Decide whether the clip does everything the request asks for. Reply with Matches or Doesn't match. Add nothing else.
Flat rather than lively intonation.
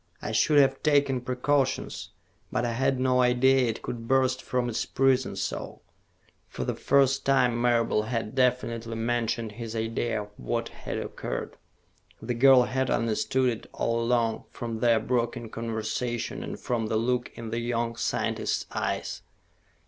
Matches